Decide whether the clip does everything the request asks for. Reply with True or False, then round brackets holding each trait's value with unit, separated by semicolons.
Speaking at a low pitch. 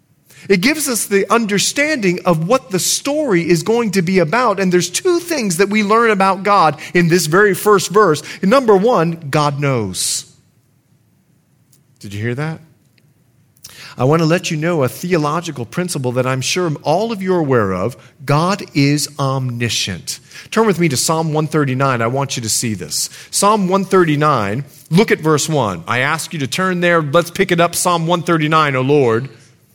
False (160 Hz)